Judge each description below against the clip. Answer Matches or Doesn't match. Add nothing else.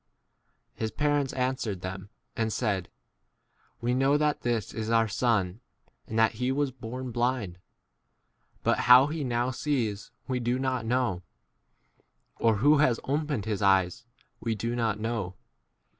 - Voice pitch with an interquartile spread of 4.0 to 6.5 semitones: Doesn't match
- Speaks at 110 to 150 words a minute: Matches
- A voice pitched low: Matches